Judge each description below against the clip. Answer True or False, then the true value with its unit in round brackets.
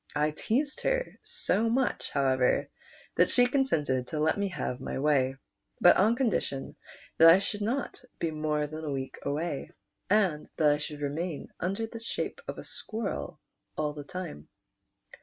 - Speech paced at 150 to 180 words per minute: True (165 wpm)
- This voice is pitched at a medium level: True (160 Hz)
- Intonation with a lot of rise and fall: True (6.7 semitones)